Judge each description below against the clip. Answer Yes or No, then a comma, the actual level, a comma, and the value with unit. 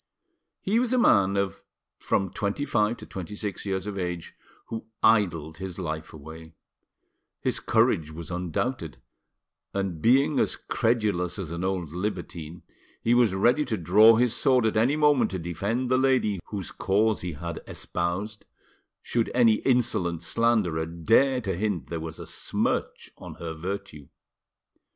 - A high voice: No, low, 100 Hz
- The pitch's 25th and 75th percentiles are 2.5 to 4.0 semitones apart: No, average, 4.9 semitones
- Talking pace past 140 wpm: Yes, average, 155 wpm